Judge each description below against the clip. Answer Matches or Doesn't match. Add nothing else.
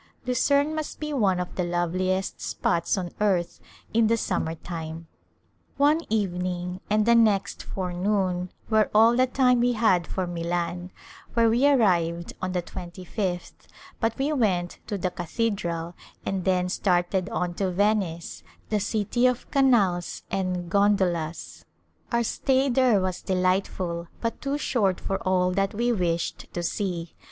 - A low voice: Doesn't match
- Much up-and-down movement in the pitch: Doesn't match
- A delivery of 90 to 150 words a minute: Doesn't match